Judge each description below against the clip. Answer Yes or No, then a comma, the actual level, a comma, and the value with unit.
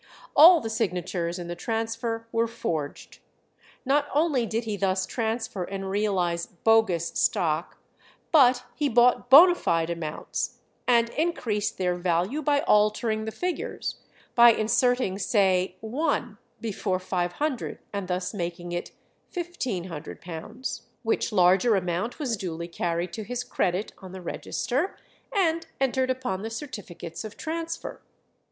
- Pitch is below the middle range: No, high, 220 Hz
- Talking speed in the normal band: No, slow, 130 wpm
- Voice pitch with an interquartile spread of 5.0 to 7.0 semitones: Yes, wide, 5.5 semitones